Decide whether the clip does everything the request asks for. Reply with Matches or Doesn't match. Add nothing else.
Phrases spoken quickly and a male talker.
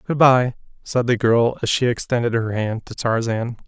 Doesn't match